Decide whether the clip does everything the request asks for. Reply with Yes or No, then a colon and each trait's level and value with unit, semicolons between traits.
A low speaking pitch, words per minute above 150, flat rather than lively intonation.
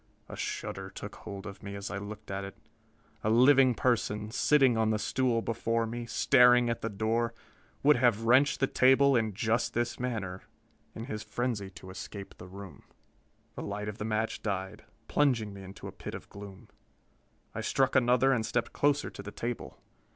No: low, 115 Hz; average, 190 wpm; average, 3.3 semitones